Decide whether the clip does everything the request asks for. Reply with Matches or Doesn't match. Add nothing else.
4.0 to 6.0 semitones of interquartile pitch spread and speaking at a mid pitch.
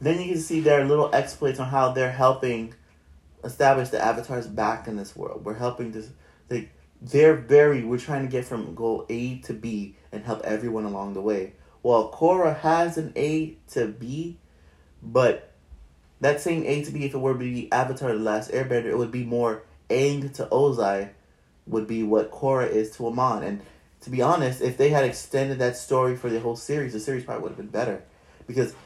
Doesn't match